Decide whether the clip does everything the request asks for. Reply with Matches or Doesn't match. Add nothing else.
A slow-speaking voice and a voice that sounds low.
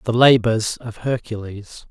Matches